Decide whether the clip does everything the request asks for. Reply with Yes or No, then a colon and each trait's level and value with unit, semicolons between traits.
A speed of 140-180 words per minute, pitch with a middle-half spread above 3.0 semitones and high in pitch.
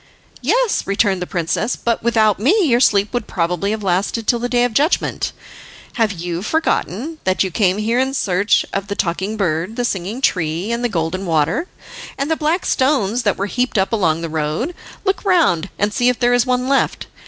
No: average, 200 wpm; average, 5.2 semitones; high, 215 Hz